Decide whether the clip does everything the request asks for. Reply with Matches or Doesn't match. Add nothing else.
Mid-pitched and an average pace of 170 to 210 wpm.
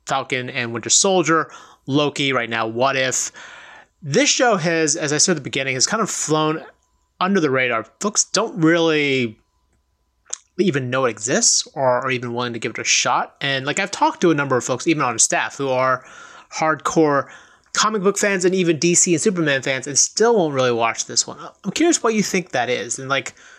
Matches